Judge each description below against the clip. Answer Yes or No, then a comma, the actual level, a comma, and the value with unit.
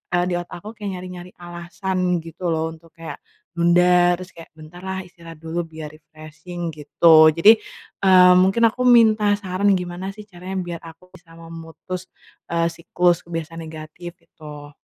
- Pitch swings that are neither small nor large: No, narrow, 2.0 semitones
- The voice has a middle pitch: Yes, medium, 175 Hz